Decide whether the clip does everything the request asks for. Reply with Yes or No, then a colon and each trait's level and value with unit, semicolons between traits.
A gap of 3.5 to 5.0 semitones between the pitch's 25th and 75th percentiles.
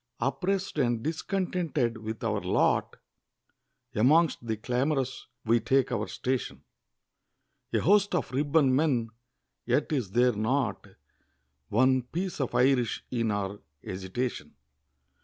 Yes: average, 4.4 semitones